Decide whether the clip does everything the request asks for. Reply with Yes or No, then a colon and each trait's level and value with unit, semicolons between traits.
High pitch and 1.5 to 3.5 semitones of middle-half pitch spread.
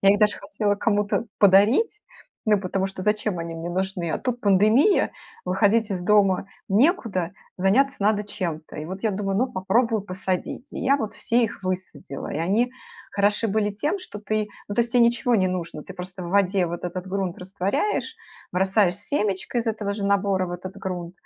Yes: high, 200 Hz; average, 2.7 semitones